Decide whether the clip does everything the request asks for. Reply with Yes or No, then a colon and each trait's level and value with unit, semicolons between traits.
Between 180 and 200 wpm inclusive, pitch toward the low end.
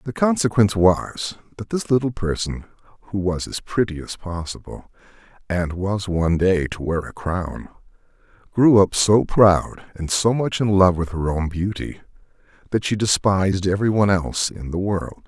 No: average, 165 wpm; very low, 95 Hz